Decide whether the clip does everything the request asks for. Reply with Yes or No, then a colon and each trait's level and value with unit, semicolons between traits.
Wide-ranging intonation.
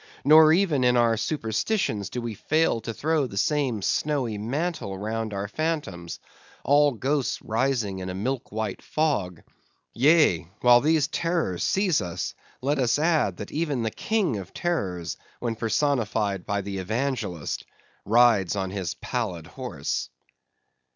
Yes: wide, 6.8 semitones